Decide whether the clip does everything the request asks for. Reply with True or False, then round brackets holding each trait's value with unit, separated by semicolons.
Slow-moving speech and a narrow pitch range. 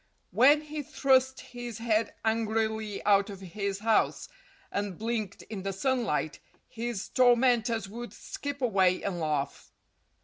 False (130 wpm; 3.6 semitones)